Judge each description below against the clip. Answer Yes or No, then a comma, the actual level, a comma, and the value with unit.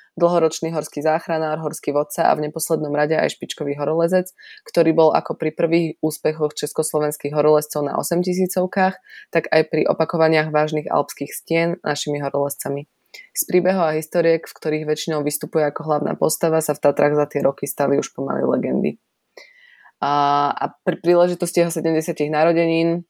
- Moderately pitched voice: Yes, medium, 155 Hz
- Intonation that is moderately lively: No, narrow, 2.2 semitones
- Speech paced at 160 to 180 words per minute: No, average, 150 wpm